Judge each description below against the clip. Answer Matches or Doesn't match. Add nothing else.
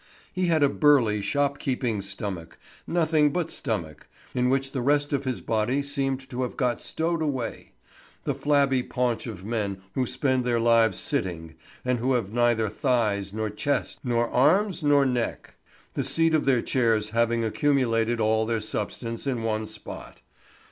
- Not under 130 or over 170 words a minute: Matches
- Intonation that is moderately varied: Matches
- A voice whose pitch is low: Matches